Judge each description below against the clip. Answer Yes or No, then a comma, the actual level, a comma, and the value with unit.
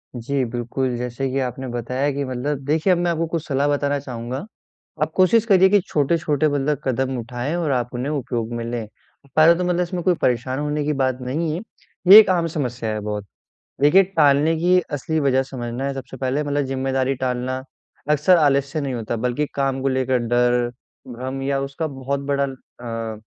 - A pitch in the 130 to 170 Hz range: Yes, low, 135 Hz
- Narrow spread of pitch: No, average, 3.3 semitones